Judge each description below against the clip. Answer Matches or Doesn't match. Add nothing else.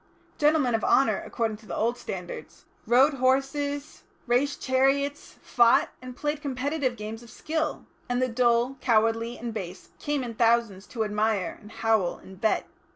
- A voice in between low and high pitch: Doesn't match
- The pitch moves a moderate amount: Matches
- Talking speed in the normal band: Matches